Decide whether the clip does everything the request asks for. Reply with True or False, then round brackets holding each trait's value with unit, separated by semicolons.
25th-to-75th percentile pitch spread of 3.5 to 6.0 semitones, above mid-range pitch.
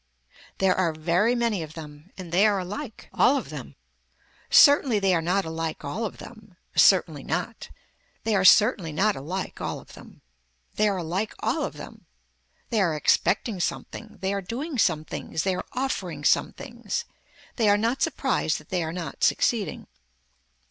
True (5.1 semitones; 195 Hz)